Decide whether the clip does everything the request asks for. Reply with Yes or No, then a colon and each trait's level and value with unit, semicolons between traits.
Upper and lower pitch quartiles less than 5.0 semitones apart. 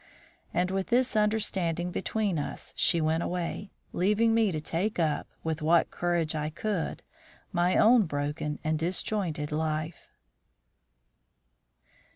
Yes: average, 4.5 semitones